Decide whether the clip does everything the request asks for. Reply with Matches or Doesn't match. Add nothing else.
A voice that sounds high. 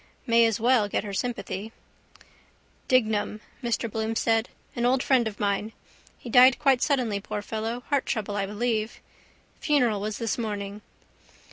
Matches